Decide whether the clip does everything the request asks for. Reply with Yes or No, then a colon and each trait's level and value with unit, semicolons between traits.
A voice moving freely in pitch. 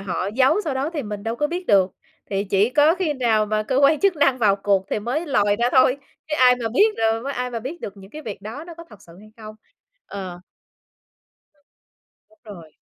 Yes: wide, 6.2 semitones